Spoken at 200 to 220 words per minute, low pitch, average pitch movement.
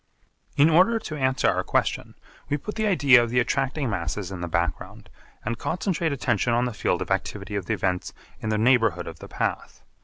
No: fast, 205 wpm; low, 120 Hz; wide, 6.3 semitones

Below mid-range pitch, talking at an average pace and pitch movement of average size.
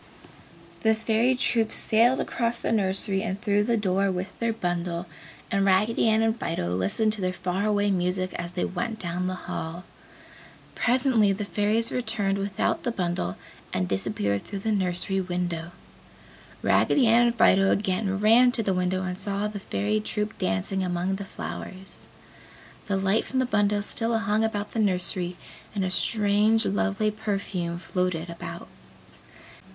No: high, 195 Hz; average, 160 wpm; average, 3.3 semitones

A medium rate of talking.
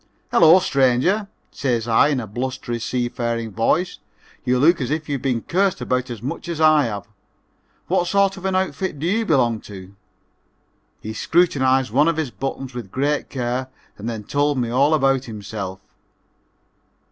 Yes: average, 170 wpm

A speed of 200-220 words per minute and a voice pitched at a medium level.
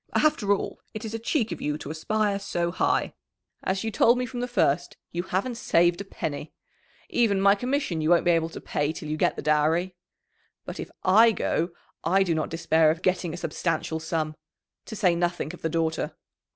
Yes: fast, 205 wpm; medium, 175 Hz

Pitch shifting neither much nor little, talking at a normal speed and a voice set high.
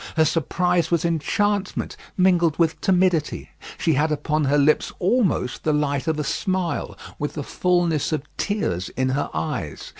No: average, 3.5 semitones; average, 155 wpm; medium, 160 Hz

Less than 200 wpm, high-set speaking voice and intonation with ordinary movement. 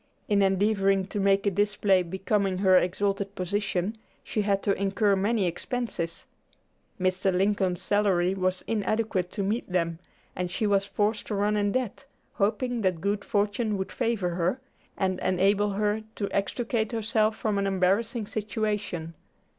No: average, 150 wpm; high, 200 Hz; narrow, 2.1 semitones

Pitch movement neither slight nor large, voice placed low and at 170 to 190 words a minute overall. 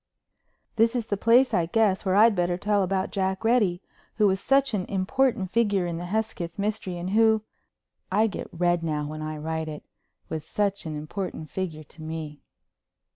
No: average, 4.5 semitones; high, 190 Hz; average, 175 wpm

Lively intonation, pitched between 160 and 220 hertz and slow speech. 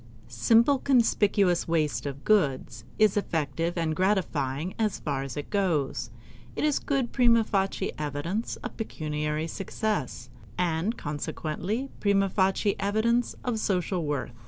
Yes: wide, 6.1 semitones; medium, 185 Hz; slow, 130 wpm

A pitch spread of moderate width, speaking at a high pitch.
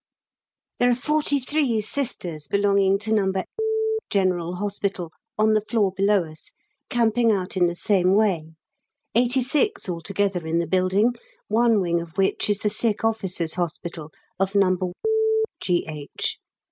Yes: average, 3.7 semitones; high, 195 Hz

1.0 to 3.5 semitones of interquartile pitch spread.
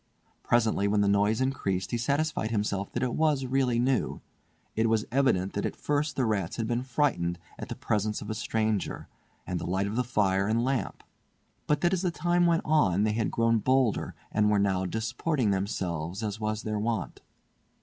No: average, 4.5 semitones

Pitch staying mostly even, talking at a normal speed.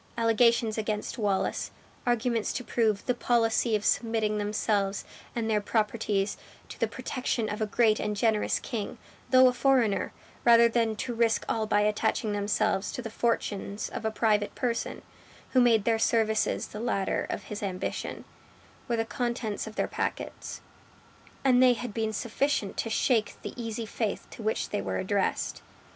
Yes: narrow, 2.0 semitones; average, 165 wpm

